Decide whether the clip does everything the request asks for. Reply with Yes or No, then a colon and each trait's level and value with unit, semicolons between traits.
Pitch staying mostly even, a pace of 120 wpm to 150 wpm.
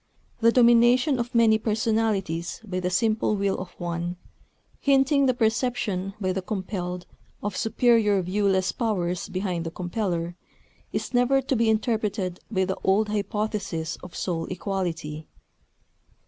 No: average, 3.9 semitones; slow, 135 wpm